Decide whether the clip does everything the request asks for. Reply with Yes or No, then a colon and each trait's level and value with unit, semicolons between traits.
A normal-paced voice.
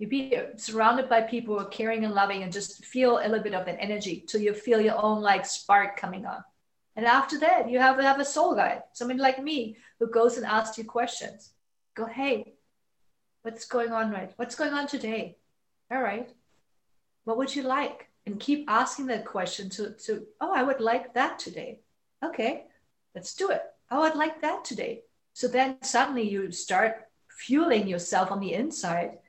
Yes: average, 195 wpm